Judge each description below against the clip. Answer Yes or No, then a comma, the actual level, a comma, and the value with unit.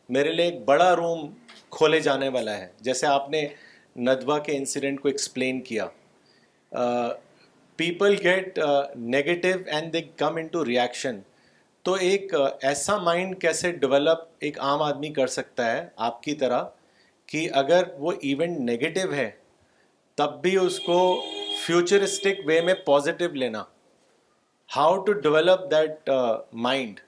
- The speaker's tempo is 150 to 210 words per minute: No, average, 135 wpm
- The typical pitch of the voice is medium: Yes, medium, 155 Hz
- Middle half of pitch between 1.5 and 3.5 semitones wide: No, average, 4.1 semitones